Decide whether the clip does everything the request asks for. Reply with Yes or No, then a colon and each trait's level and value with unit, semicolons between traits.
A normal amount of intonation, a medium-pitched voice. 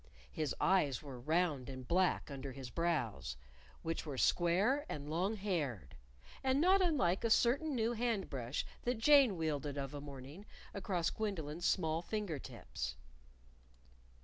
No: wide, 7.4 semitones; medium, 170 Hz